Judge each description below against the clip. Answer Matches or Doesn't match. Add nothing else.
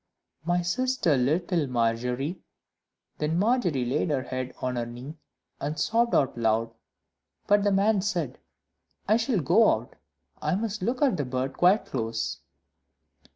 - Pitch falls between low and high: Matches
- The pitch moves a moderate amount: Doesn't match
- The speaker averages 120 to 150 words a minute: Matches